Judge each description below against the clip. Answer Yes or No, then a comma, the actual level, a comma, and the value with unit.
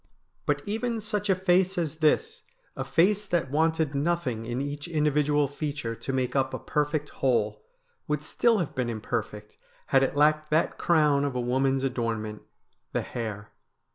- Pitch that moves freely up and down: No, average, 4.0 semitones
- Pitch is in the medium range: Yes, medium, 145 Hz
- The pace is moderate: Yes, average, 170 wpm